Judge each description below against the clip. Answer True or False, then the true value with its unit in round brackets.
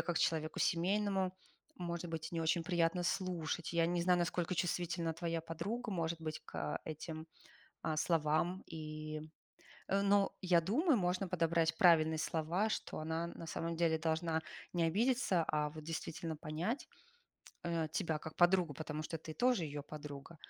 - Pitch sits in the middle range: True (165 Hz)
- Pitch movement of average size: False (2.1 semitones)